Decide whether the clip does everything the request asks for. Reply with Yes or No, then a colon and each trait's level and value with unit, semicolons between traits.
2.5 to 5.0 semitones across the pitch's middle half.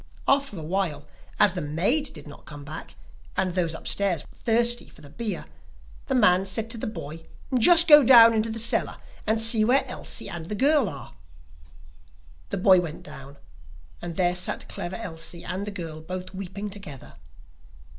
No: wide, 5.4 semitones